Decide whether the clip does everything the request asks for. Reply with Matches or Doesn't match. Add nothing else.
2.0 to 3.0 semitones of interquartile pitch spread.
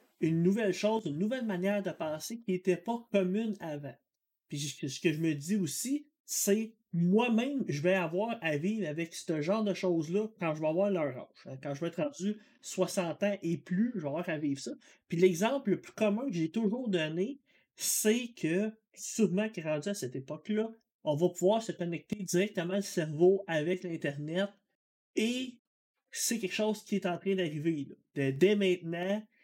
Doesn't match